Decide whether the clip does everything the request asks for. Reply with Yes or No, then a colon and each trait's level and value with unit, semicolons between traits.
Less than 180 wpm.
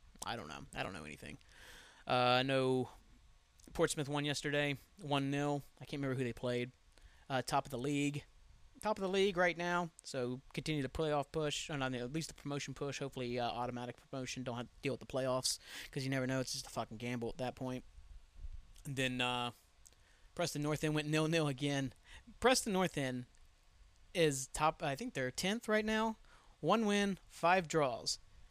No: average, 190 wpm